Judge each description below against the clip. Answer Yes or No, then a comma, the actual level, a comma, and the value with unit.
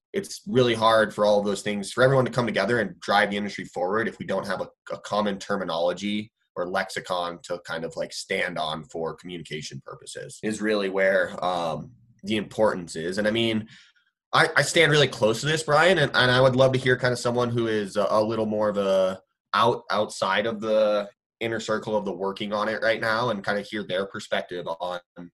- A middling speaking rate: No, fast, 220 wpm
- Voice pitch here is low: Yes, low, 105 Hz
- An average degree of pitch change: Yes, average, 3.0 semitones